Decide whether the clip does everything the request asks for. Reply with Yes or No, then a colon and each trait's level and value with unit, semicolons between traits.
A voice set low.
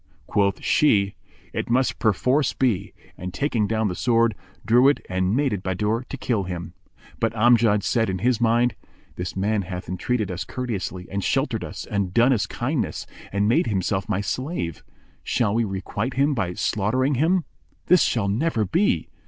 Yes: low, 110 Hz